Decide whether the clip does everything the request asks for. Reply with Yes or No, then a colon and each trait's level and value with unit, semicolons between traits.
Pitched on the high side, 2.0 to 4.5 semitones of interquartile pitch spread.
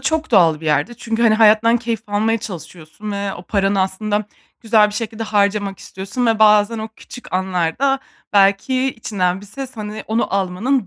Yes: high, 210 Hz; average, 2.8 semitones